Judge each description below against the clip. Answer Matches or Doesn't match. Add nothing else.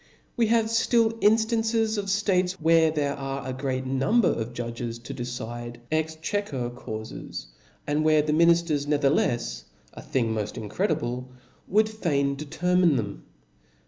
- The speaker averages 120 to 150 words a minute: Matches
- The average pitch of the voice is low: Doesn't match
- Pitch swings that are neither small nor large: Doesn't match